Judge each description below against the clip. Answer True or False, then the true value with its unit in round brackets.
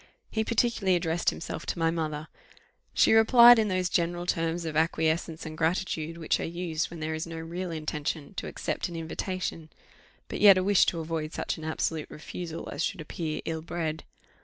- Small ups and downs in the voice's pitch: True (2.2 semitones)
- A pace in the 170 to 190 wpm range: True (185 wpm)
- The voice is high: False (165 Hz)